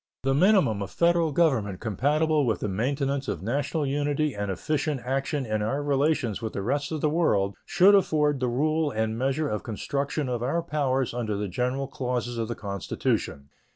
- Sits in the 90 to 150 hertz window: Yes, low, 135 Hz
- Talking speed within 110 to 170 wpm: No, average, 185 wpm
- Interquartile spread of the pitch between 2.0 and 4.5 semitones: No, average, 5.1 semitones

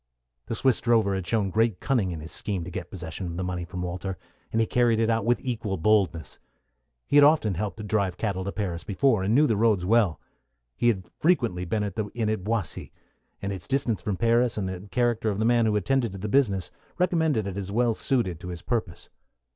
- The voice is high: No, low, 105 Hz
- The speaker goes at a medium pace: No, fast, 225 wpm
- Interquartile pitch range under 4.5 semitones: Yes, average, 3.9 semitones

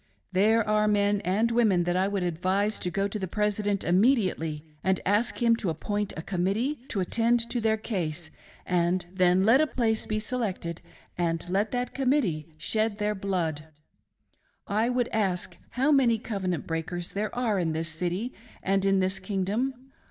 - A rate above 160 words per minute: Yes, average, 180 wpm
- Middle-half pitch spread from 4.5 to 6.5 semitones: No, average, 3.9 semitones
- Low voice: No, high, 200 Hz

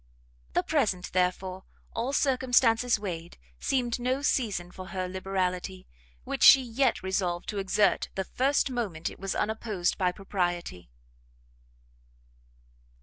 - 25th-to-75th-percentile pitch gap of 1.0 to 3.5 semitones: No, average, 4.8 semitones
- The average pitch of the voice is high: Yes, high, 195 Hz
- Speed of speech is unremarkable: No, slow, 120 wpm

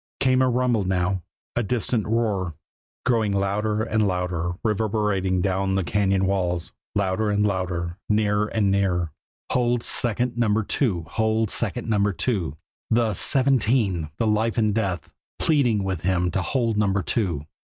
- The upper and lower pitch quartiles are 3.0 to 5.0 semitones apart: Yes, average, 3.3 semitones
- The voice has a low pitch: Yes, low, 105 Hz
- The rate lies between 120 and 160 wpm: Yes, average, 145 wpm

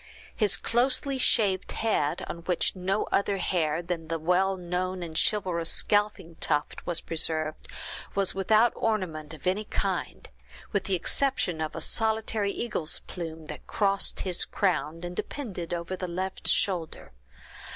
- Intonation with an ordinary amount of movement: Yes, average, 3.6 semitones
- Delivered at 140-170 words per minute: Yes, average, 145 wpm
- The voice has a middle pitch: Yes, medium, 180 Hz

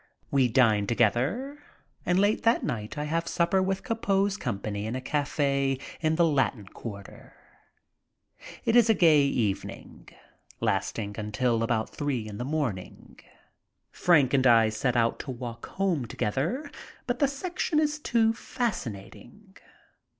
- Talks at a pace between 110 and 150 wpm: Yes, average, 145 wpm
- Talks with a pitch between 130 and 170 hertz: Yes, medium, 140 Hz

